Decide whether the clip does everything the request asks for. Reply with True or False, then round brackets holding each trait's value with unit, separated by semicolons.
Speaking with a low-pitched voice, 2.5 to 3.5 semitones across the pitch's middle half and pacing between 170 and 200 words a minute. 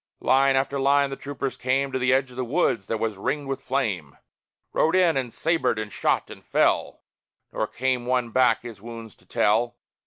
True (130 Hz; 2.8 semitones; 195 wpm)